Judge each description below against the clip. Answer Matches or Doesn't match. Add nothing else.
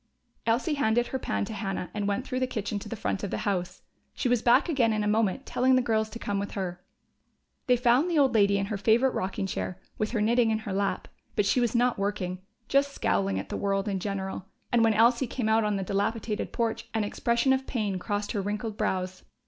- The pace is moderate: Doesn't match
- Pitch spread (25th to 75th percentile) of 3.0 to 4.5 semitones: Matches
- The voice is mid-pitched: Doesn't match